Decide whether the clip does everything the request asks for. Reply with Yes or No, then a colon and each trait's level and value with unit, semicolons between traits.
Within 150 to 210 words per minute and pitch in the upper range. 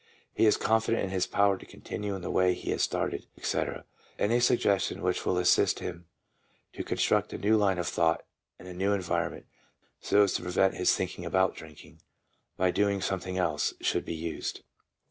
No: average, 190 wpm; very low, 95 Hz